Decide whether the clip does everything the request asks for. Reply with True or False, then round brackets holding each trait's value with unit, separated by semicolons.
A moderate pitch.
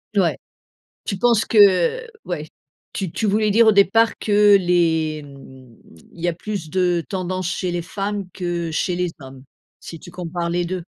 True (180 Hz)